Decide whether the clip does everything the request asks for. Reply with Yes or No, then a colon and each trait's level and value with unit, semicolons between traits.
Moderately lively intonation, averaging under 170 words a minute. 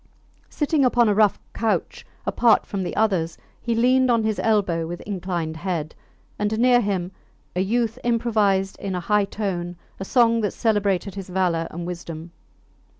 Yes: average, 4.2 semitones; average, 160 wpm